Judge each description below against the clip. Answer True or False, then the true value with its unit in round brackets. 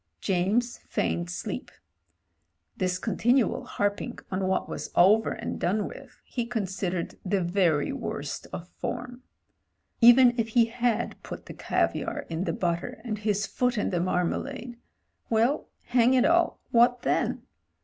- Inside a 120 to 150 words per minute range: True (145 wpm)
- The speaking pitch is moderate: False (215 Hz)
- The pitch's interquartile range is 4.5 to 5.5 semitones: True (4.9 semitones)